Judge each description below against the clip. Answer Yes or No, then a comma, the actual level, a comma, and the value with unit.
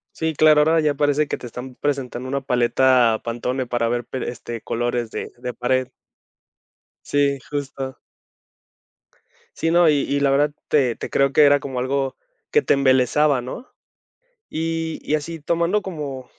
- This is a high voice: No, medium, 140 Hz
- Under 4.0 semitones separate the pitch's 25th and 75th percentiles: Yes, average, 3.2 semitones